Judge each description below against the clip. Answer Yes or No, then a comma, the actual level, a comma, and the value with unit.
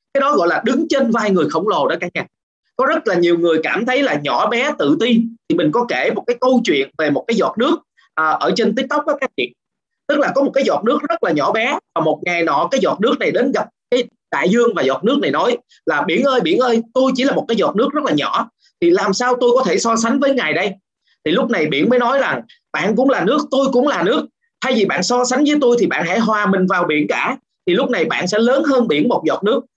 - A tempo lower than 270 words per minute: No, fast, 280 wpm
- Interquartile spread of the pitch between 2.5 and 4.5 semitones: Yes, average, 3.7 semitones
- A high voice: Yes, very high, 250 Hz